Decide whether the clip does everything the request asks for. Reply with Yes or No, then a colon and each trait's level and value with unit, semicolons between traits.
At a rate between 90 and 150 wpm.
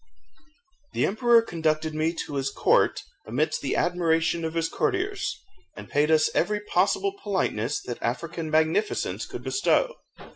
Yes: average, 140 wpm